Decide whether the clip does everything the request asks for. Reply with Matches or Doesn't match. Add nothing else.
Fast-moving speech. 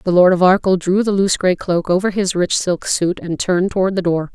Matches